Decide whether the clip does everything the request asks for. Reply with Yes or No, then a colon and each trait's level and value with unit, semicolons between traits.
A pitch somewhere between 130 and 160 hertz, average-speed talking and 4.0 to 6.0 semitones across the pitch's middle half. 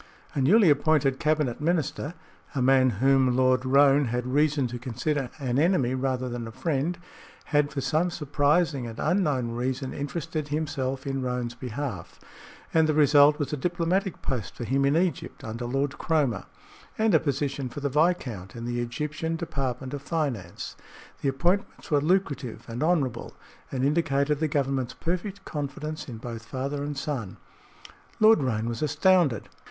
No: medium, 140 Hz; average, 160 wpm; average, 3.4 semitones